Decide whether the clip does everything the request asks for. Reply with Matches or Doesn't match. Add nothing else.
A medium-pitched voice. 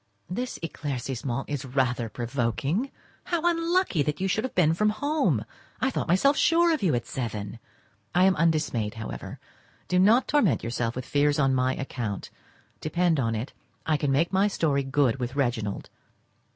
Matches